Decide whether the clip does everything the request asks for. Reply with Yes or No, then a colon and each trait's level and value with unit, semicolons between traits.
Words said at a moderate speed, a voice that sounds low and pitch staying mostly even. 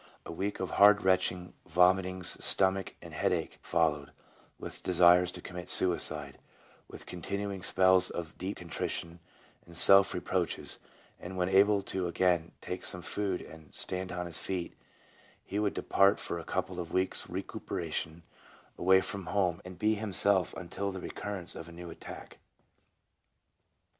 Yes: average, 150 wpm; very low, 90 Hz; narrow, 1.8 semitones